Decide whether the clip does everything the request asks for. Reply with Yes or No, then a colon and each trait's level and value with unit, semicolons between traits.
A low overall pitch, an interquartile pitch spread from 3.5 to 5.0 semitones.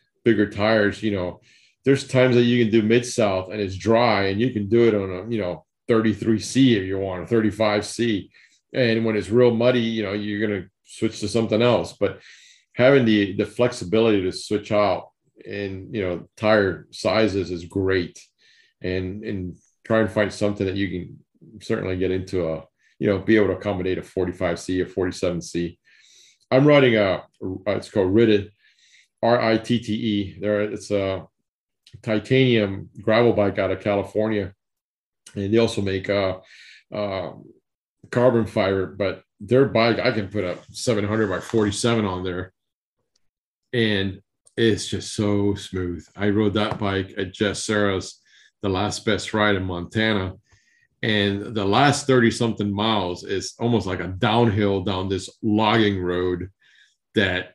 No: low, 105 Hz; average, 2.8 semitones